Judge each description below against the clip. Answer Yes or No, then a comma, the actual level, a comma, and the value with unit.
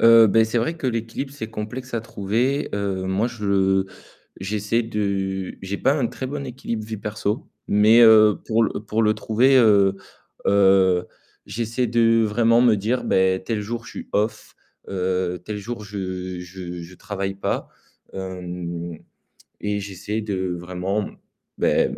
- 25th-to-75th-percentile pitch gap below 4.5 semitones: Yes, average, 3.2 semitones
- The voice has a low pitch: Yes, low, 105 Hz